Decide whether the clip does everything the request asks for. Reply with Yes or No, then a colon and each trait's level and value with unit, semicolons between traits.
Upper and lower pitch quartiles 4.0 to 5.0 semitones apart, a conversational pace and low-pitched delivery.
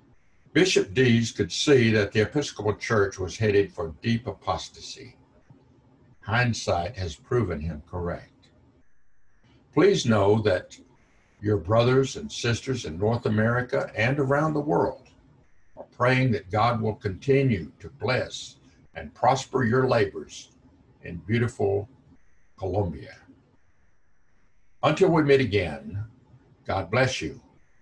No: average, 4.3 semitones; slow, 115 wpm; low, 110 Hz